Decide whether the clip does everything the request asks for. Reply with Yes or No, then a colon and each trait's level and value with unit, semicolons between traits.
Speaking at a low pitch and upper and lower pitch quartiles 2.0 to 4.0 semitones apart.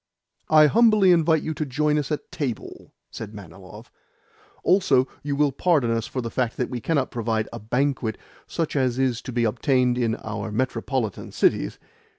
No: low, 130 Hz; average, 4.7 semitones